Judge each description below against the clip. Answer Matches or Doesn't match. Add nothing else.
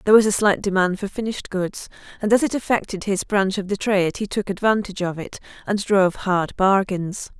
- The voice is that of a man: Doesn't match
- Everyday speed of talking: Doesn't match